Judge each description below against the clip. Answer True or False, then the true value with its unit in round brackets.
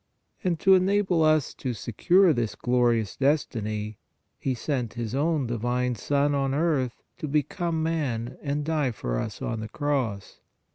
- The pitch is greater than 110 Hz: True (135 Hz)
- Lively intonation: False (4.9 semitones)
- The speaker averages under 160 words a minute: True (150 wpm)